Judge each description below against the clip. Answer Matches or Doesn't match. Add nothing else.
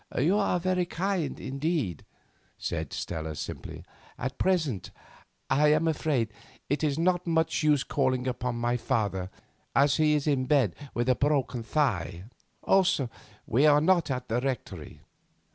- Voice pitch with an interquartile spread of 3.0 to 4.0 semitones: Doesn't match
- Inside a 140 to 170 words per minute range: Matches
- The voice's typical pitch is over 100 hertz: Matches